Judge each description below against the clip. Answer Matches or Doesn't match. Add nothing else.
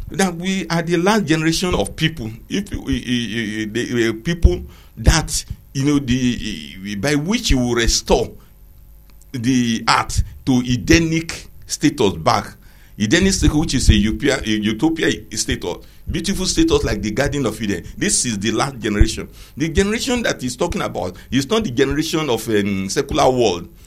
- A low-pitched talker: Matches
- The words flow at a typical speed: Matches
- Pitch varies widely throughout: Matches